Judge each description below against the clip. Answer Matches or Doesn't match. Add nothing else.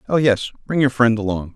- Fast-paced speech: Matches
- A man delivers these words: Matches